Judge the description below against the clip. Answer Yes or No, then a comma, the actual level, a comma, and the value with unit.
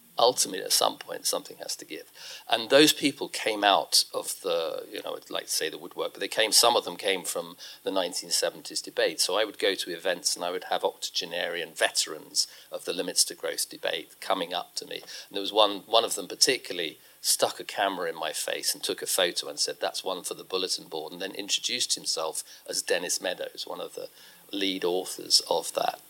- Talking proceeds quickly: Yes, fast, 220 wpm